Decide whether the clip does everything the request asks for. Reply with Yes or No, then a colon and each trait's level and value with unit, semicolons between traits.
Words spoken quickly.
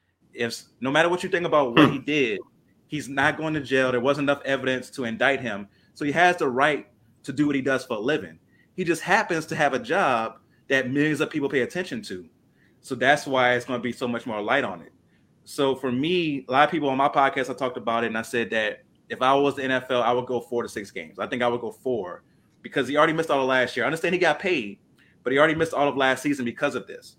Yes: fast, 270 wpm